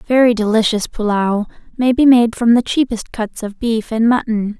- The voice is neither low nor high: No, high, 225 Hz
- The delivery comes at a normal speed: Yes, average, 185 wpm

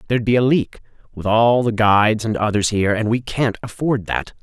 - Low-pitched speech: Yes, low, 115 Hz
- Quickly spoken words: Yes, fast, 215 wpm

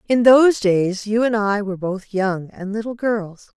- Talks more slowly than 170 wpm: No, average, 200 wpm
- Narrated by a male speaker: No, female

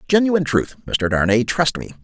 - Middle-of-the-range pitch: Yes, medium, 145 Hz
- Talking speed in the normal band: Yes, average, 175 wpm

